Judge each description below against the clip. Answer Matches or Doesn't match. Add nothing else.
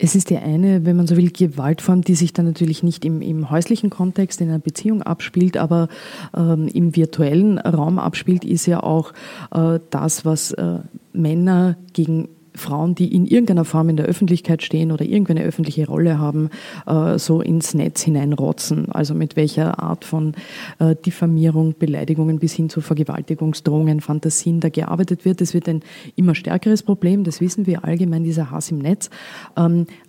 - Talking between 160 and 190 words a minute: Matches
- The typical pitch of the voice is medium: Matches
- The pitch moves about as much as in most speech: Doesn't match